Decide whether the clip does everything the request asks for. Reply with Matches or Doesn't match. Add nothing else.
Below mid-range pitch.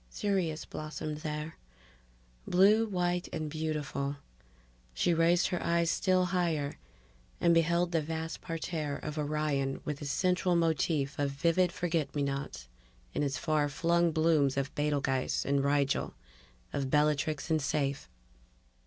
Doesn't match